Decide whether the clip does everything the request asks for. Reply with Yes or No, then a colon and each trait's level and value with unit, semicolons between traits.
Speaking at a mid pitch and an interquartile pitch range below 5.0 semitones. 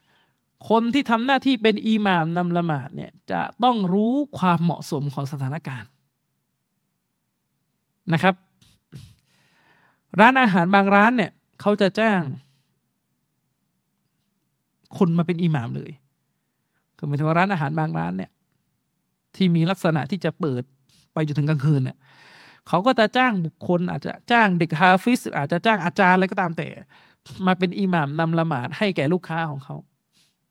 Yes: medium, 175 Hz; average, 4.6 semitones